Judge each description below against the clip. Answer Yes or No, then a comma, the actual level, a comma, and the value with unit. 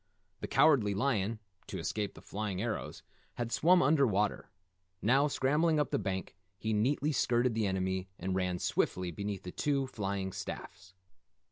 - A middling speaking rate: Yes, average, 155 wpm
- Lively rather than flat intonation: Yes, wide, 5.9 semitones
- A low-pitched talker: Yes, low, 105 Hz